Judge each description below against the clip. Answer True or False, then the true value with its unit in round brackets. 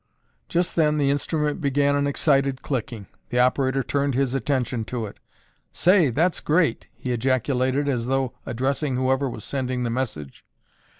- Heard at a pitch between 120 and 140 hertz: True (135 Hz)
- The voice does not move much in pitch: True (2.3 semitones)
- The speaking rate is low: False (155 wpm)